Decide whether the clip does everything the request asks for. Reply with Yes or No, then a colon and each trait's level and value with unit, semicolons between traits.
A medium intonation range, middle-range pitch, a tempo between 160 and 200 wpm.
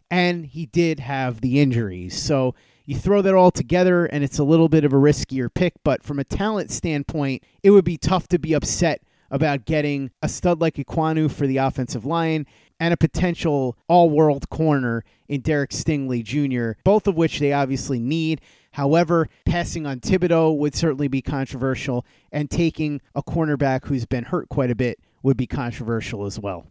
Yes: average, 3.7 semitones; medium, 145 Hz; average, 185 wpm